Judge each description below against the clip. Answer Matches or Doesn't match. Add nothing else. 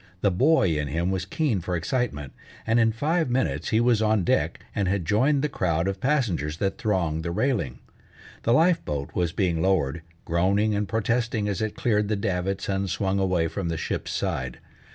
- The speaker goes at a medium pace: Matches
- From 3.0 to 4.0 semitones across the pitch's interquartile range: Doesn't match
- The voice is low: Matches